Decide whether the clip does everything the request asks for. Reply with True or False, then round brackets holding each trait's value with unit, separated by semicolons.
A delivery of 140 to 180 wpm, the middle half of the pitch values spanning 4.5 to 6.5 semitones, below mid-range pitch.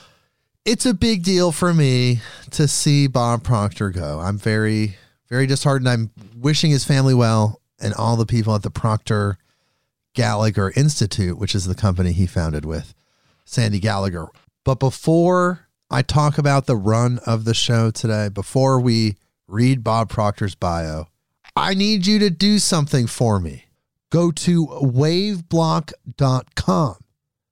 True (145 wpm; 5.6 semitones; 120 Hz)